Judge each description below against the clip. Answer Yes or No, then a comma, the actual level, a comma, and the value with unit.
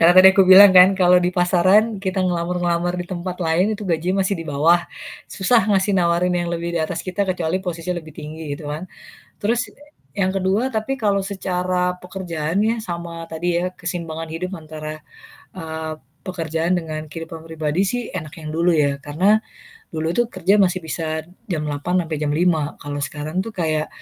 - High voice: No, medium, 175 Hz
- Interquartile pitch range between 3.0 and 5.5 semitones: No, narrow, 2.6 semitones